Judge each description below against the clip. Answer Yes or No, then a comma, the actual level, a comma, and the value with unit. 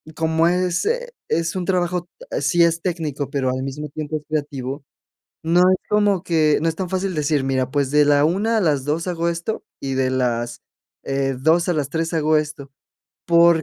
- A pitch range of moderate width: Yes, average, 3.6 semitones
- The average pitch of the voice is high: No, medium, 160 Hz